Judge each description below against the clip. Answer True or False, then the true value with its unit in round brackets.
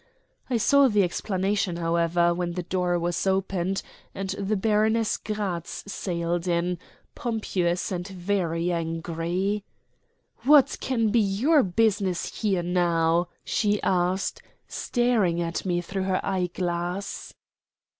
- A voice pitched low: False (185 Hz)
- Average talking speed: False (115 wpm)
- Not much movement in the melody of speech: False (3.0 semitones)